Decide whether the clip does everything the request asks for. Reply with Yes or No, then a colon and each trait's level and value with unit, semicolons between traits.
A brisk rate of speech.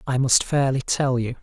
Yes: fast, 210 wpm